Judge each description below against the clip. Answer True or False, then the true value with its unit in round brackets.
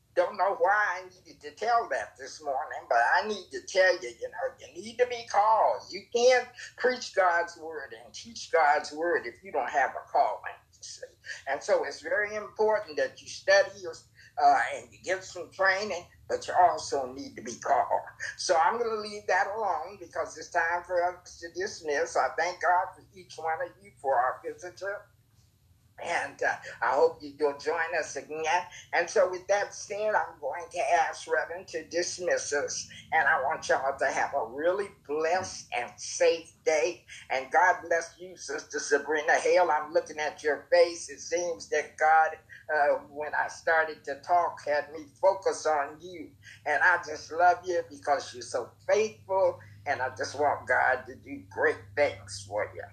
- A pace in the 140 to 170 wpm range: False (185 wpm)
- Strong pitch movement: True (5.7 semitones)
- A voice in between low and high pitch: True (175 Hz)